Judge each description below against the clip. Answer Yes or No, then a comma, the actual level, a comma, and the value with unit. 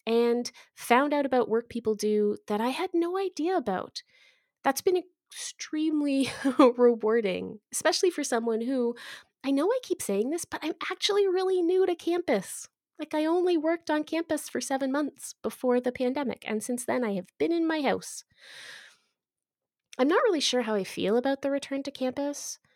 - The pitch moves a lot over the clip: Yes, wide, 5.8 semitones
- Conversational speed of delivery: Yes, average, 175 wpm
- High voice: Yes, very high, 280 Hz